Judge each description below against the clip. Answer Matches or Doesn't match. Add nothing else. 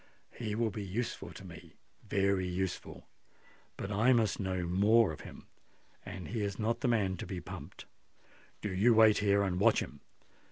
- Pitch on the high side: Doesn't match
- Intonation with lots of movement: Doesn't match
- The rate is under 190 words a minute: Matches